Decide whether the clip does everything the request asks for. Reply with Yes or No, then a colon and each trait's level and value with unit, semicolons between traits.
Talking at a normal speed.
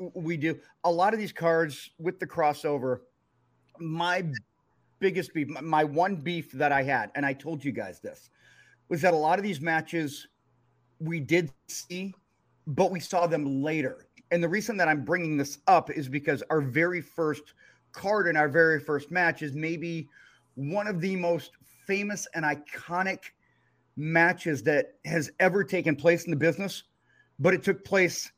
Yes: average, 170 wpm